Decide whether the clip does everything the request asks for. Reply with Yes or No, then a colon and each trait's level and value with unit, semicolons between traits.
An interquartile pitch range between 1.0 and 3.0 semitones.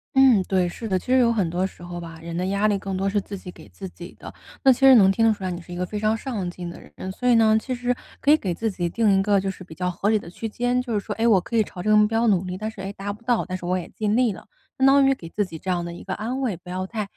No: average, 3.8 semitones